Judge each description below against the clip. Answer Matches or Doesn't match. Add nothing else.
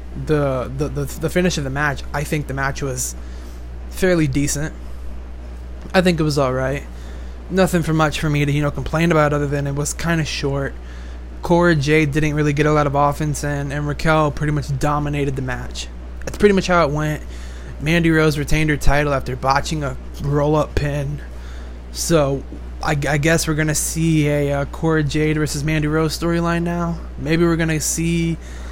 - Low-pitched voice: Doesn't match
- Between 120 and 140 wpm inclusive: Doesn't match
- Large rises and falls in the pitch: Doesn't match